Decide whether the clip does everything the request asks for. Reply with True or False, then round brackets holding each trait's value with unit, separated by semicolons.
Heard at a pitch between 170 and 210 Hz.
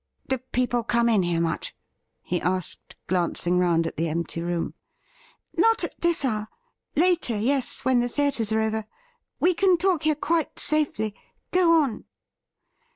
False (235 Hz)